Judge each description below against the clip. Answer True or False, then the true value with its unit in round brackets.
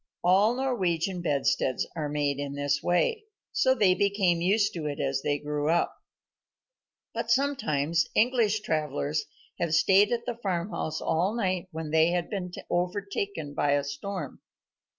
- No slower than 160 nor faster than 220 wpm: False (150 wpm)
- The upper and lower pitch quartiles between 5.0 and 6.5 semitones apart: True (5.3 semitones)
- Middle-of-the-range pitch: True (175 Hz)